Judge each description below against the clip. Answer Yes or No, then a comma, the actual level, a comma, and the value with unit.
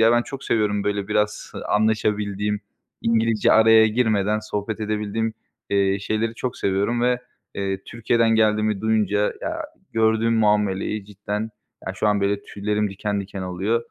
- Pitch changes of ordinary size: No, narrow, 1.7 semitones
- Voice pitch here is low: Yes, low, 105 Hz